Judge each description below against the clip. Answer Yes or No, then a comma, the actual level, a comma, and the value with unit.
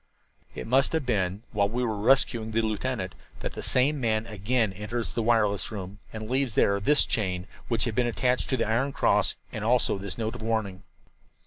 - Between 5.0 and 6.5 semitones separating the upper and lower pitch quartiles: No, average, 3.4 semitones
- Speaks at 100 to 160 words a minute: No, average, 200 wpm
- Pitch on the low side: Yes, low, 110 Hz